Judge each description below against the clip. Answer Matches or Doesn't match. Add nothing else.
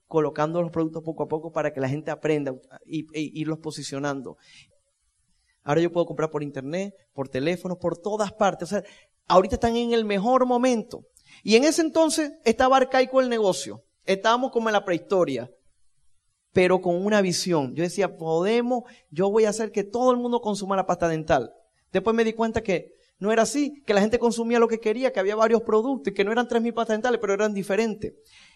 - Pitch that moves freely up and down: Matches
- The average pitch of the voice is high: Matches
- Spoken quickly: Matches